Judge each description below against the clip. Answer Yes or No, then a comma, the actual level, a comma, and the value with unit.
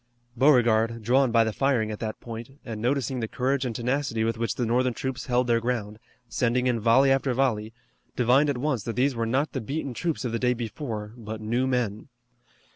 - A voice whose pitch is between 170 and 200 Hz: No, low, 120 Hz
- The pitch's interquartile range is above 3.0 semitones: No, narrow, 2.6 semitones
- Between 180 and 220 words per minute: Yes, fast, 205 wpm